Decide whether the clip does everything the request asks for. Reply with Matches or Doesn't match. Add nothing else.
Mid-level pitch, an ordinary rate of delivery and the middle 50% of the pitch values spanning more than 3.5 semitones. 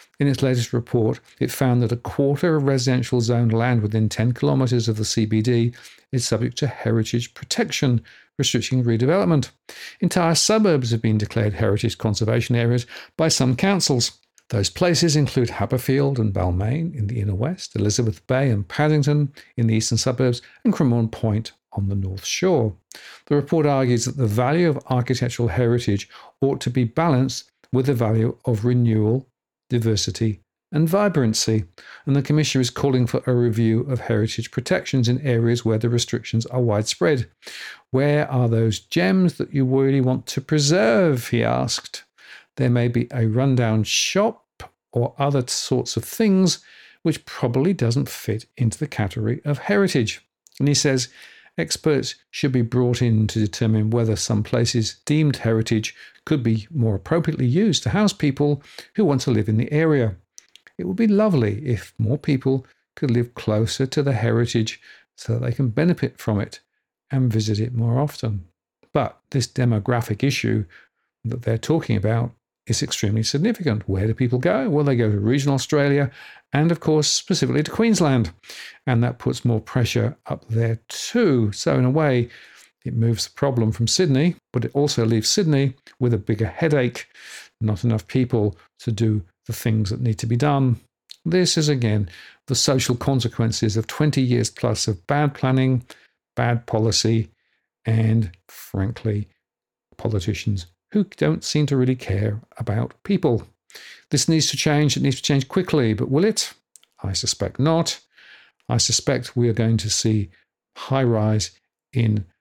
Doesn't match